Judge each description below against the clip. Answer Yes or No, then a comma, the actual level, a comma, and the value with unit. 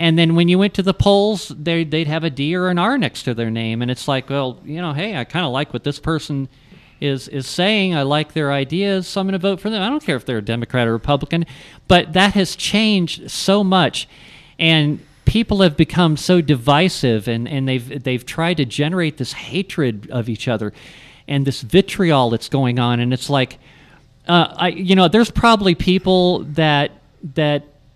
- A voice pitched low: No, medium, 155 Hz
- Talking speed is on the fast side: Yes, fast, 210 wpm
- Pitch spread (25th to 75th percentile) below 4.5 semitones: No, wide, 5.4 semitones